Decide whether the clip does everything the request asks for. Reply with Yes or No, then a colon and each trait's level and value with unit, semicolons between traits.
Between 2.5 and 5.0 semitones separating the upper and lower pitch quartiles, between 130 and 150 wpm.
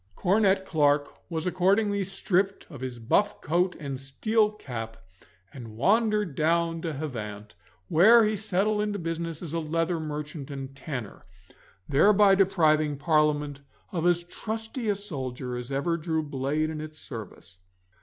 No: wide, 5.5 semitones; average, 145 wpm